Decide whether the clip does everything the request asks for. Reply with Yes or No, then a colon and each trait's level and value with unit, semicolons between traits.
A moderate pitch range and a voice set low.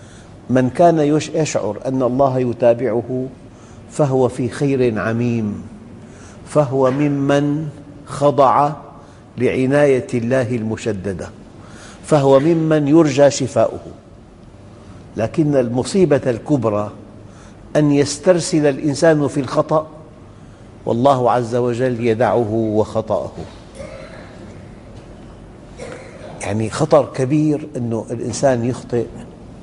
Yes: average, 3.9 semitones; low, 130 Hz